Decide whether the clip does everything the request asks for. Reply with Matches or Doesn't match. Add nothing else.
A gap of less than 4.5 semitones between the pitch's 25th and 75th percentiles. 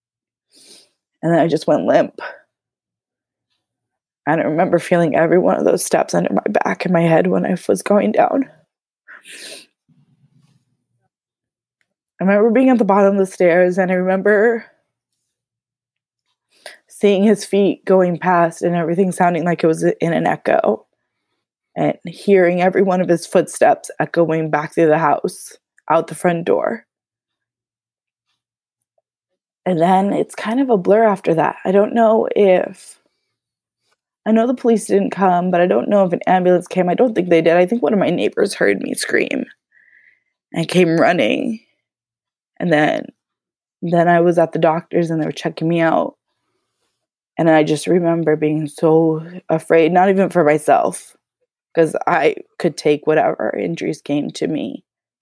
Matches